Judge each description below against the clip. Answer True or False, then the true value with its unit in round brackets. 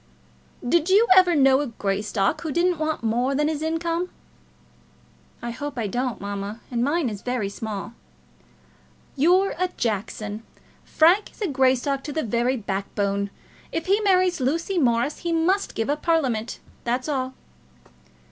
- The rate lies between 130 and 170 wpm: True (145 wpm)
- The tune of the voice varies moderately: False (6.5 semitones)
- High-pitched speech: True (265 Hz)